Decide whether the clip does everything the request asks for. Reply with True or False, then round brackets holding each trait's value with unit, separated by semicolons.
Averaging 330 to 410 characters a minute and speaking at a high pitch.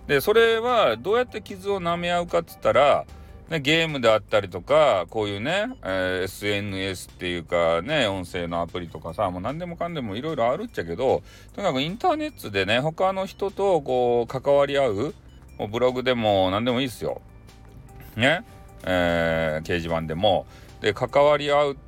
False (360 characters per minute; 120 Hz)